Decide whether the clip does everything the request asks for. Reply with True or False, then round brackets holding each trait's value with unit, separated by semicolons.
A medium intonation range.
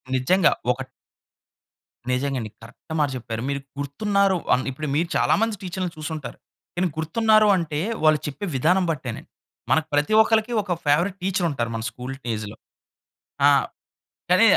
False (6.2 semitones)